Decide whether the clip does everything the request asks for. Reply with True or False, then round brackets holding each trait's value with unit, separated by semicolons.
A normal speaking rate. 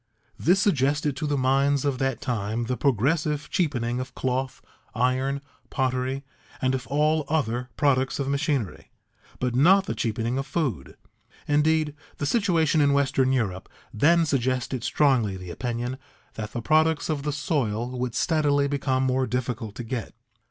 True (150 wpm)